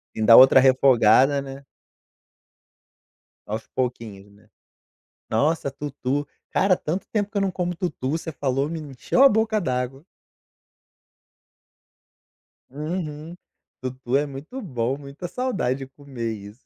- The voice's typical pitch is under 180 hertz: Yes, medium, 140 Hz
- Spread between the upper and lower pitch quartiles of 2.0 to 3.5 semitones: No, average, 4.5 semitones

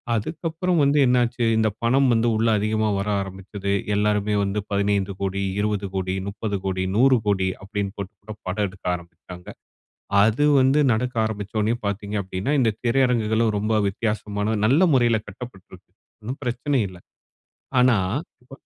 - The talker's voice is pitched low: Yes, low, 105 Hz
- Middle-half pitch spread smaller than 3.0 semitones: No, average, 3.4 semitones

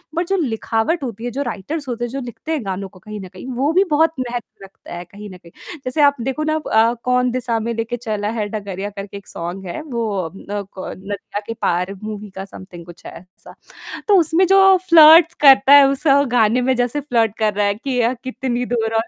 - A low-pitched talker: No, high, 230 Hz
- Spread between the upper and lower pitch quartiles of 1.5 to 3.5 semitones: No, average, 5.2 semitones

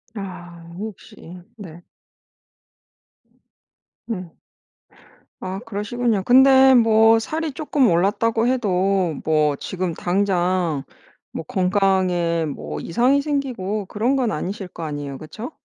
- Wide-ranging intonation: No, average, 4.9 semitones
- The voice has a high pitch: Yes, high, 195 Hz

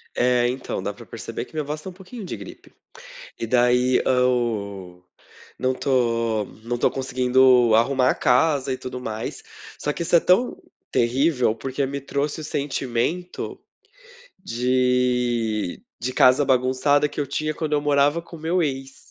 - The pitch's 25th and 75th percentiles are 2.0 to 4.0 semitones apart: Yes, average, 3.1 semitones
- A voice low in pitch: Yes, low, 130 Hz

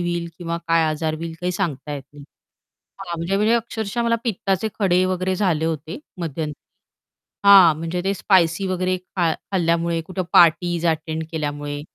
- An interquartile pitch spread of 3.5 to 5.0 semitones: No, narrow, 2.6 semitones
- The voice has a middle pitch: Yes, medium, 170 Hz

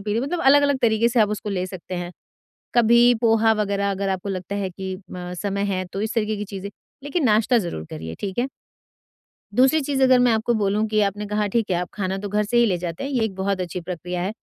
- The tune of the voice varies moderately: Yes, average, 3.7 semitones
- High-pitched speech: Yes, high, 205 Hz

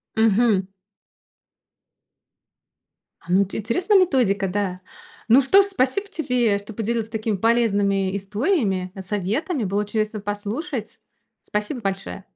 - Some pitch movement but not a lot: Yes, average, 3.9 semitones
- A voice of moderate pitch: No, high, 215 Hz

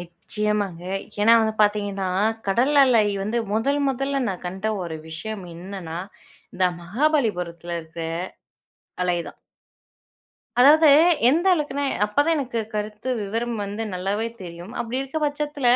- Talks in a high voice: Yes, high, 210 Hz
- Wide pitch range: Yes, wide, 6.2 semitones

